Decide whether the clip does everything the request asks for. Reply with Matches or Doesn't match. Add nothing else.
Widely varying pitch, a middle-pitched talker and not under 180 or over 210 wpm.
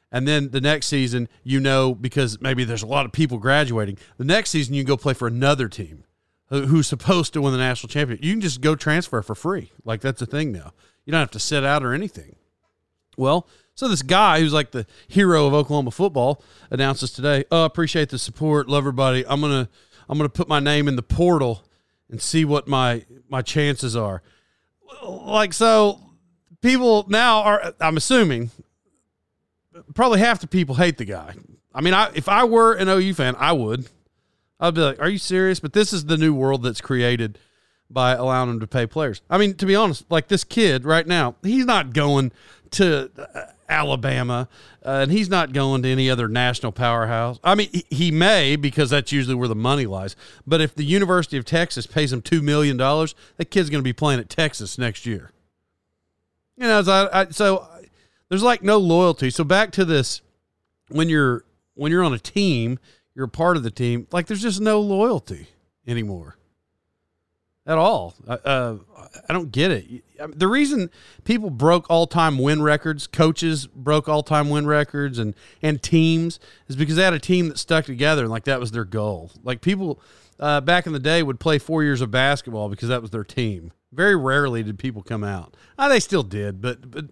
Matches